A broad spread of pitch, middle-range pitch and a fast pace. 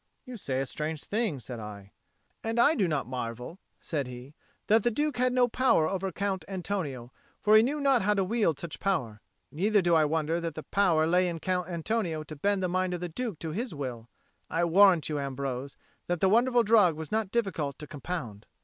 Yes: wide, 5.9 semitones; medium, 175 Hz; fast, 210 wpm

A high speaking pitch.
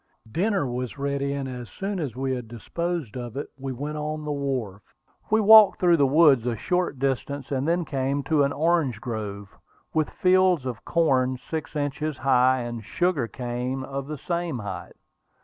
No: medium, 140 Hz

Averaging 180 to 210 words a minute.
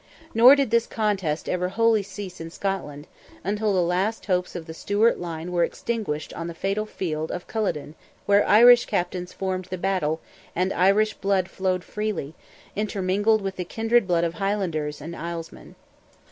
No: average, 165 wpm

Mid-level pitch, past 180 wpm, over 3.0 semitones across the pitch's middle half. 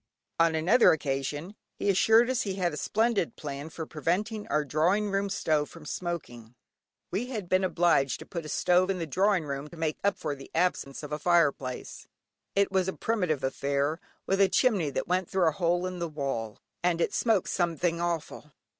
Yes: medium, 170 Hz; average, 200 wpm; average, 4.2 semitones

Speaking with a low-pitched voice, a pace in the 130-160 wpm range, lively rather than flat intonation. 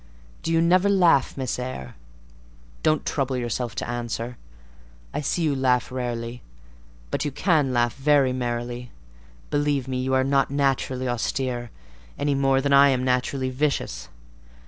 No: low, 130 Hz; average, 145 wpm; narrow, 2.6 semitones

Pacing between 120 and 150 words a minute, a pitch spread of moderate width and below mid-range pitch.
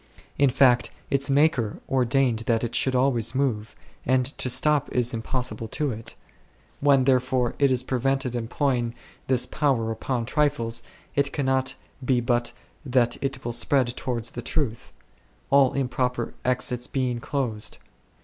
No: average, 140 wpm; narrow, 2.3 semitones; low, 125 Hz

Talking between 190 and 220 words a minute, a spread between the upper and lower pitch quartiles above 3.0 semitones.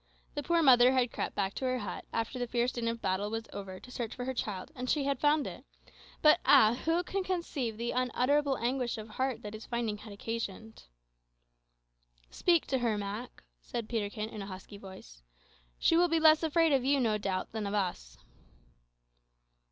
Yes: average, 195 wpm; average, 4.6 semitones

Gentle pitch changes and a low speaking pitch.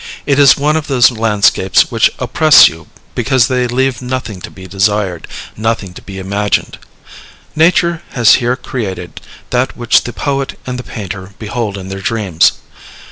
No: average, 5.0 semitones; low, 115 Hz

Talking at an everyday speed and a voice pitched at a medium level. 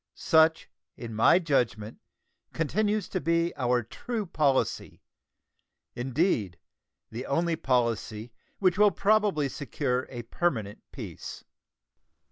No: slow, 100 wpm; medium, 145 Hz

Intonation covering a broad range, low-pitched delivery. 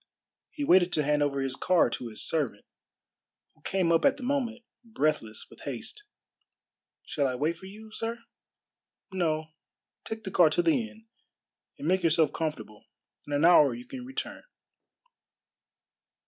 No: wide, 6.9 semitones; medium, 170 Hz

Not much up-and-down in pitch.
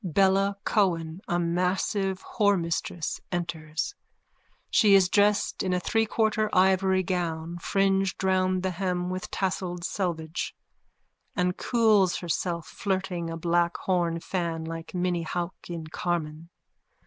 Yes: narrow, 2.2 semitones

